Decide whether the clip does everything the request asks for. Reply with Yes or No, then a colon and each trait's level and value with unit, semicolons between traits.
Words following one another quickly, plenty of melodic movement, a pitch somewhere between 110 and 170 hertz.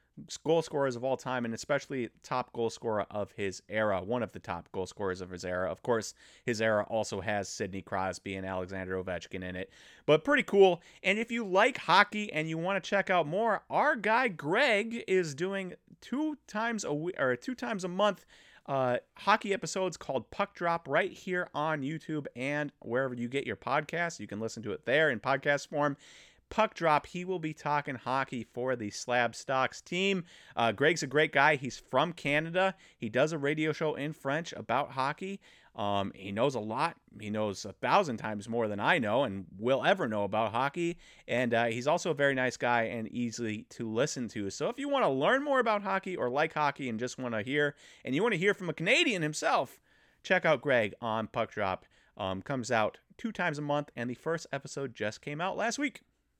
Yes: fast, 210 wpm; wide, 7.6 semitones; medium, 140 Hz